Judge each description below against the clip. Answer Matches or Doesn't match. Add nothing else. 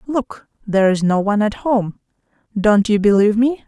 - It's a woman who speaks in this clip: Matches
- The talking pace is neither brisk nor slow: Matches